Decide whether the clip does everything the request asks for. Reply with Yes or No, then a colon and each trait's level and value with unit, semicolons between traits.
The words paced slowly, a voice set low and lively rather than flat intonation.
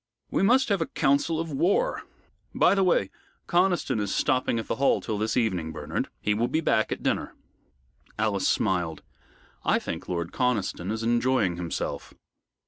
No: average, 165 wpm; low, 115 Hz; wide, 8.2 semitones